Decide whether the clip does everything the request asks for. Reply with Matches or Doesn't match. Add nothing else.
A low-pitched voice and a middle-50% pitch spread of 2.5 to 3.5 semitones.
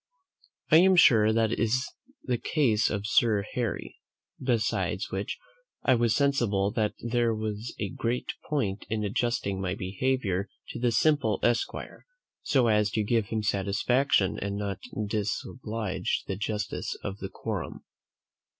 Matches